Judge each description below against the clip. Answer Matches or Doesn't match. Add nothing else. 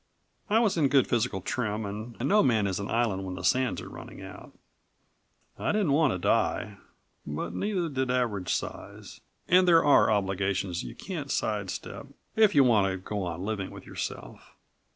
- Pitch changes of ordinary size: Doesn't match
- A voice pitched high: Doesn't match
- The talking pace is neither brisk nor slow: Matches